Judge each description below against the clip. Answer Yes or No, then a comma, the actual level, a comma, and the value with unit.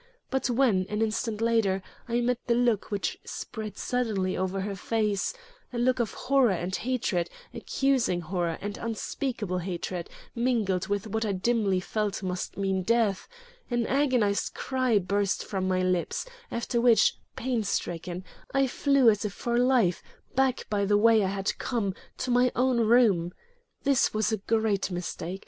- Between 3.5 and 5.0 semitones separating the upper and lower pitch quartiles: Yes, average, 4.1 semitones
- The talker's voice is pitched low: No, high, 215 Hz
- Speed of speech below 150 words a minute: No, average, 160 wpm